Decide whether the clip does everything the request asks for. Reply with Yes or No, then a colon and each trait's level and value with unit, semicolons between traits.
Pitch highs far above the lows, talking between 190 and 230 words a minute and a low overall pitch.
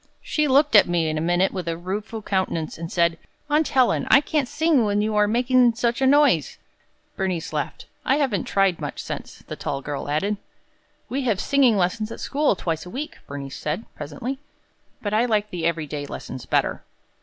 No: wide, 7.0 semitones; average, 195 wpm; high, 205 Hz